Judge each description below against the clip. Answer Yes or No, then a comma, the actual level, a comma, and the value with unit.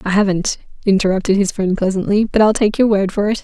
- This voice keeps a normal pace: No, fast, 225 wpm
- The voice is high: Yes, high, 200 Hz